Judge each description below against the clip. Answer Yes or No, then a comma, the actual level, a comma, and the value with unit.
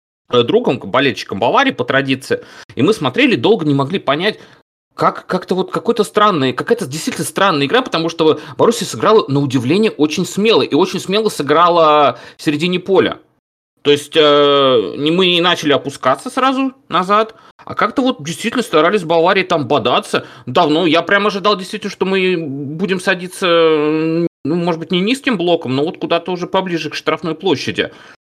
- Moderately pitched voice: Yes, medium, 170 Hz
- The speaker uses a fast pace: Yes, fast, 165 wpm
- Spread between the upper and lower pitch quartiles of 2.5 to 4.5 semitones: No, average, 4.9 semitones